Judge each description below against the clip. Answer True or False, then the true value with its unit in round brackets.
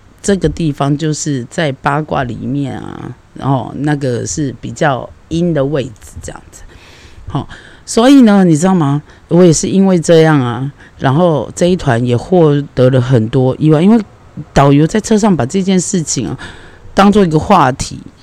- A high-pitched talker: False (150 Hz)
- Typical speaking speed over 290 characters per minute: False (245 characters per minute)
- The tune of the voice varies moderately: False (5.7 semitones)